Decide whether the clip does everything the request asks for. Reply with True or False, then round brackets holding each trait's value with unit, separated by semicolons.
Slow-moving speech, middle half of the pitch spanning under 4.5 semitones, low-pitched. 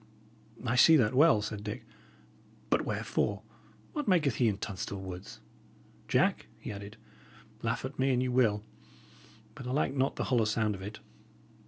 False (165 wpm; 4.1 semitones; 115 Hz)